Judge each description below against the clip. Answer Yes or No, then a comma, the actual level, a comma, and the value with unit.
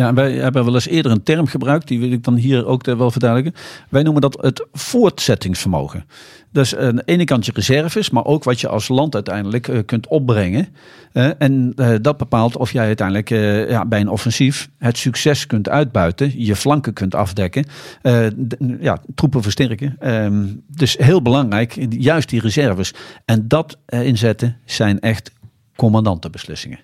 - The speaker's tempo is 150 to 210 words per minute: Yes, average, 155 wpm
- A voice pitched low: Yes, low, 125 Hz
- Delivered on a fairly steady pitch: No, average, 3.9 semitones